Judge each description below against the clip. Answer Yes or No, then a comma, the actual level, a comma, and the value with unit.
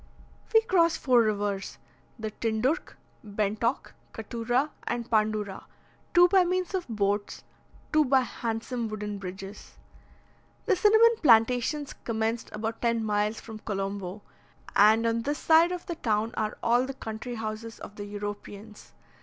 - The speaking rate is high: No, slow, 135 wpm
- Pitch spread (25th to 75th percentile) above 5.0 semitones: No, average, 3.9 semitones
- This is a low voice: No, high, 225 Hz